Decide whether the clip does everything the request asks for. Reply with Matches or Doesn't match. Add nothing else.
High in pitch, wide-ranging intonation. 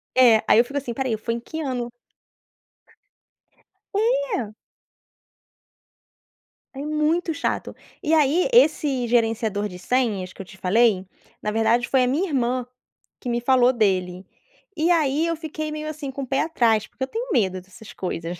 Matches